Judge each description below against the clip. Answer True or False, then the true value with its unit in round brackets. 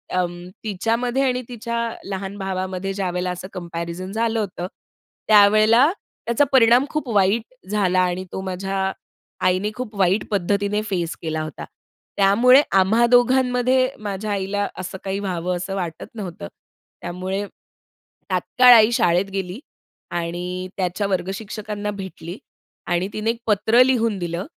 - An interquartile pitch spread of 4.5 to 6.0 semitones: False (3.5 semitones)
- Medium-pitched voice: False (195 Hz)